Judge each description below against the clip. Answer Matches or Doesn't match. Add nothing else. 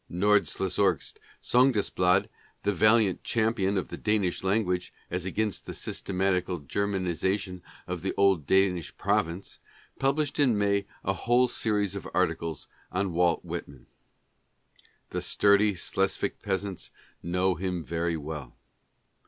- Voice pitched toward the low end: Matches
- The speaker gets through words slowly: Matches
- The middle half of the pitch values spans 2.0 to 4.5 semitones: Matches